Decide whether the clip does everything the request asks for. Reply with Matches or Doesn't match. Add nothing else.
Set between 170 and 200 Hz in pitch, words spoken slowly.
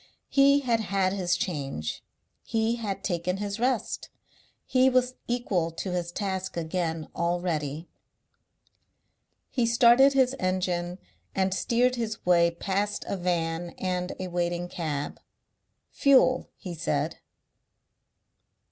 Matches